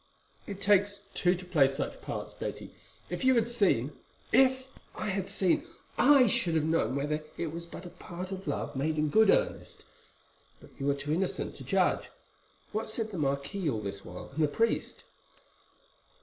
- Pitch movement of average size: No, wide, 6.0 semitones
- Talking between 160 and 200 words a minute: Yes, average, 180 wpm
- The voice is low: No, medium, 175 Hz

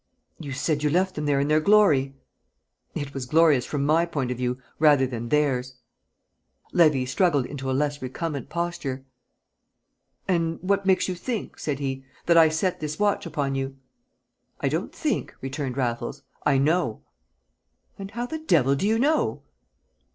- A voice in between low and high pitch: Yes, medium, 150 Hz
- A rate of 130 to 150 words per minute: No, average, 165 wpm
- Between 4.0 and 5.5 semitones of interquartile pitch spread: Yes, average, 4.4 semitones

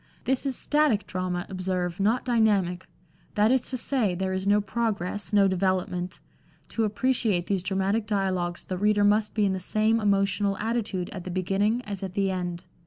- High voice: Yes, high, 200 Hz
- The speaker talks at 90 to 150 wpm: No, average, 175 wpm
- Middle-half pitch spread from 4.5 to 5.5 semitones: No, average, 2.7 semitones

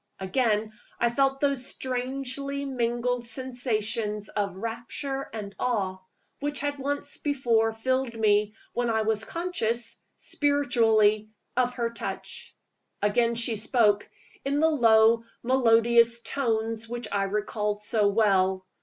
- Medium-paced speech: No, slow, 120 wpm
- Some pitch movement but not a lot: Yes, average, 3.3 semitones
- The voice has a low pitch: No, high, 235 Hz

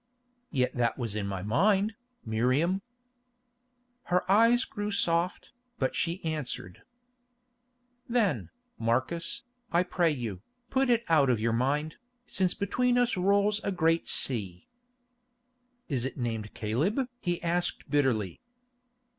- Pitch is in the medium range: Yes, medium, 165 Hz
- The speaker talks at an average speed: No, slow, 120 wpm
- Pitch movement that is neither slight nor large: No, wide, 8.6 semitones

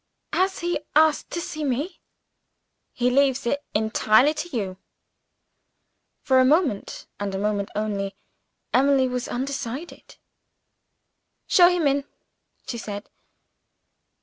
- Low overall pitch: No, very high, 260 Hz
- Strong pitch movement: Yes, wide, 5.9 semitones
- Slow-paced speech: Yes, slow, 115 wpm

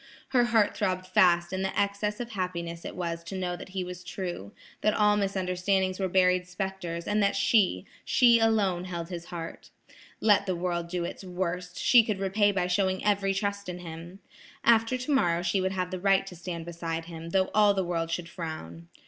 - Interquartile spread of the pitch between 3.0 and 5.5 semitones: No, narrow, 2.6 semitones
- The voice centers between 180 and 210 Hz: Yes, medium, 185 Hz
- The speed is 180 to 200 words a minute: Yes, average, 195 wpm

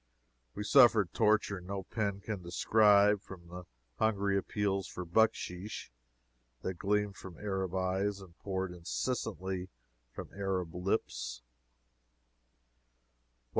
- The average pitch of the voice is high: No, very low, 95 Hz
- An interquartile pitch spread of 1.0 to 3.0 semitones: Yes, narrow, 2.4 semitones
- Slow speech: Yes, slow, 105 wpm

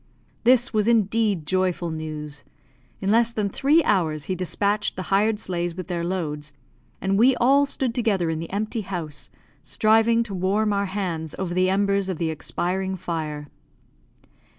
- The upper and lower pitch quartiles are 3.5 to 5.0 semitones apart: Yes, average, 4.2 semitones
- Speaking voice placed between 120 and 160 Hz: No, high, 190 Hz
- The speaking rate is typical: Yes, average, 160 wpm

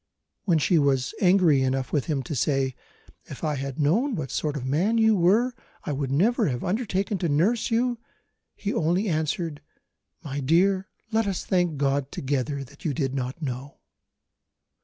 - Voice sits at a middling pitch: Yes, medium, 155 Hz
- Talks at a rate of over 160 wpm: Yes, average, 170 wpm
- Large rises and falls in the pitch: Yes, wide, 5.8 semitones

